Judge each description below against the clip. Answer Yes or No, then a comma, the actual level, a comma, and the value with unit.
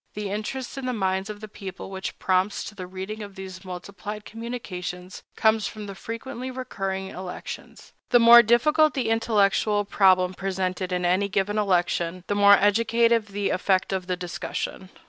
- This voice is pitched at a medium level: No, high, 200 Hz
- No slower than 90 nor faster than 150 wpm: No, average, 165 wpm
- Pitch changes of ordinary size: Yes, average, 3.0 semitones